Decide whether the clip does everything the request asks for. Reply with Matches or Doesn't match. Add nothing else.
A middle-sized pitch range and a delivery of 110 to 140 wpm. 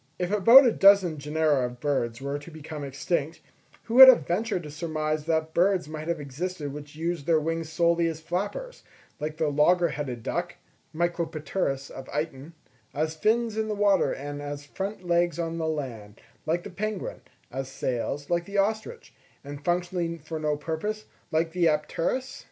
Doesn't match